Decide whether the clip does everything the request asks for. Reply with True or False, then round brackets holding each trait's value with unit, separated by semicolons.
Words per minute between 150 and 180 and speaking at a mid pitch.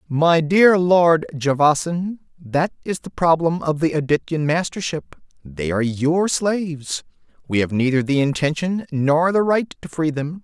True (155 wpm; 160 Hz)